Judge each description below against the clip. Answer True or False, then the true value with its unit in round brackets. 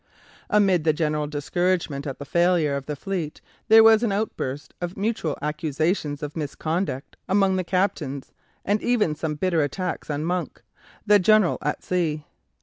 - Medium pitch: True (170 Hz)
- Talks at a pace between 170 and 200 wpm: False (155 wpm)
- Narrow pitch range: False (4.3 semitones)